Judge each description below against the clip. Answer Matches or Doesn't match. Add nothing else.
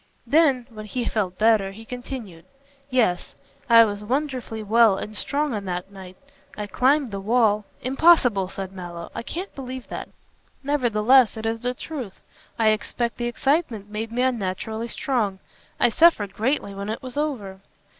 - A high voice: Matches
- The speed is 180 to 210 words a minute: Doesn't match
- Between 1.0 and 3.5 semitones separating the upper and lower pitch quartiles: Doesn't match